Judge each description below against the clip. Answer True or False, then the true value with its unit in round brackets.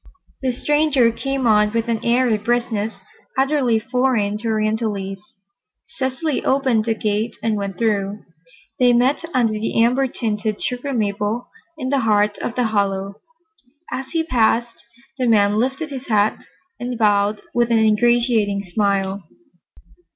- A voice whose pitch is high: True (225 Hz)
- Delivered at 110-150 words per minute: True (140 wpm)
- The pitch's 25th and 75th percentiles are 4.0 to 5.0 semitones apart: False (3.2 semitones)